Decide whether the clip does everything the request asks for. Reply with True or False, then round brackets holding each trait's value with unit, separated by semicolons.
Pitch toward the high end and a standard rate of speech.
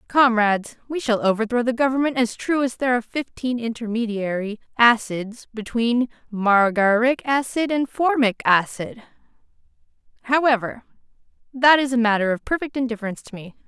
False (235 Hz; 130 wpm)